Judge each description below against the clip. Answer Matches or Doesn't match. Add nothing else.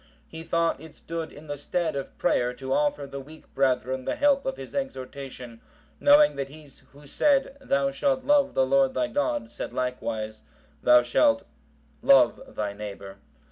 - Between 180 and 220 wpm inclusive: Doesn't match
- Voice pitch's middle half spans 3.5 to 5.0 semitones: Doesn't match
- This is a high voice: Doesn't match